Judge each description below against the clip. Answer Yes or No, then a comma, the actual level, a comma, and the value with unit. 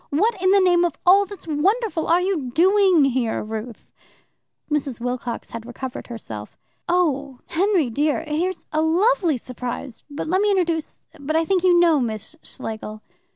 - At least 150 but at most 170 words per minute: Yes, average, 160 wpm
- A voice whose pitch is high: Yes, very high, 315 Hz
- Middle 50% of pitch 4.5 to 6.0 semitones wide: No, wide, 6.6 semitones